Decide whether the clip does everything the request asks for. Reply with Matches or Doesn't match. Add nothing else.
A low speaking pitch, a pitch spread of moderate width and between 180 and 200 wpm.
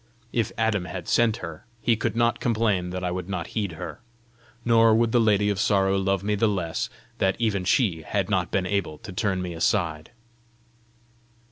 Matches